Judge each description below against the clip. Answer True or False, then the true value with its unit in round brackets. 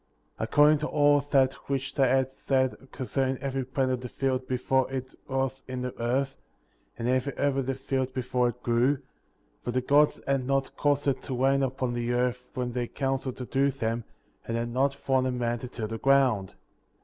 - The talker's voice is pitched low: True (130 Hz)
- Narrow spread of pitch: True (1.6 semitones)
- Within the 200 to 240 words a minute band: True (205 wpm)